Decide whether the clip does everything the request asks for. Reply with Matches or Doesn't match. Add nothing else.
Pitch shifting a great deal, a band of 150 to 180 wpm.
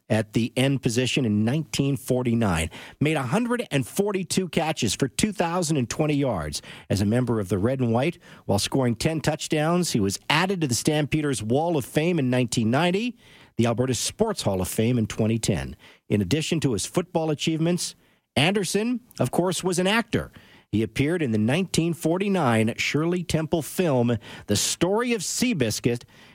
Matches